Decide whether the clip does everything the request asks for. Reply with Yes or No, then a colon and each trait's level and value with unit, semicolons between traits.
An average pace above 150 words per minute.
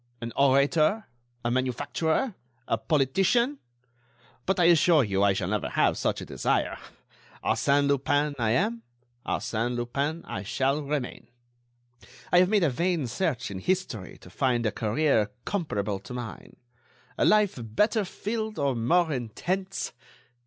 No: average, 140 wpm